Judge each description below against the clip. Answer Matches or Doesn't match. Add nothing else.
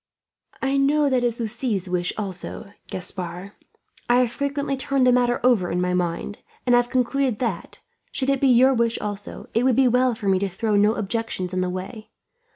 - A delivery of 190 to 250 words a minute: Matches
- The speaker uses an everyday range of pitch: Matches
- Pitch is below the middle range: Doesn't match